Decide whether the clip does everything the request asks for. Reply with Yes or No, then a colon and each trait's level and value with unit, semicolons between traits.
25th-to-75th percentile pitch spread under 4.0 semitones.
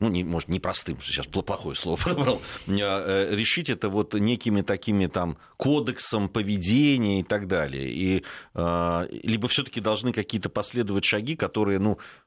Yes: average, 3.4 semitones